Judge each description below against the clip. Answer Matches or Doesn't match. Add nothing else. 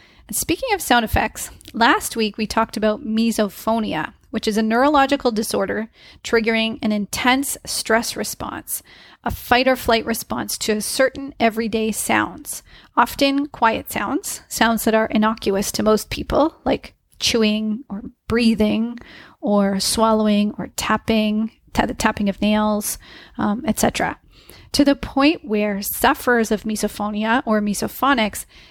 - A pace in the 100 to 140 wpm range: Matches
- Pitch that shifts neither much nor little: Doesn't match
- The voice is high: Matches